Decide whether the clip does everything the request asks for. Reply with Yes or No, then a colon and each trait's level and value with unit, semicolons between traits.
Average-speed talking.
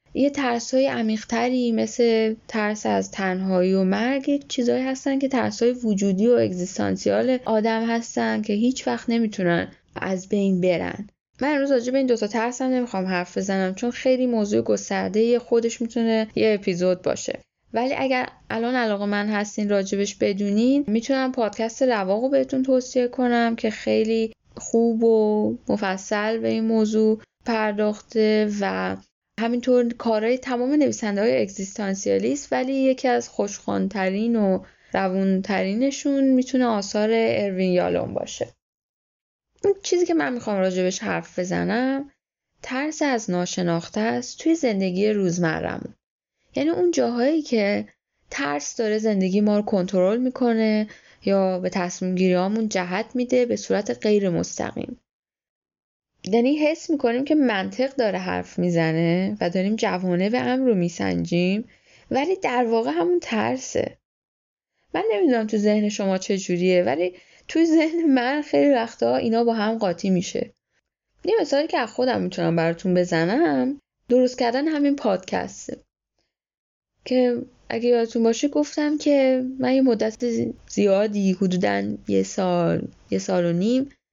Yes: average, 135 wpm